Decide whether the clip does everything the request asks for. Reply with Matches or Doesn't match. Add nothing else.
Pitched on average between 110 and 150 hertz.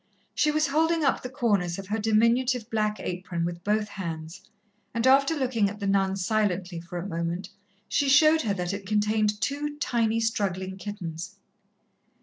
Doesn't match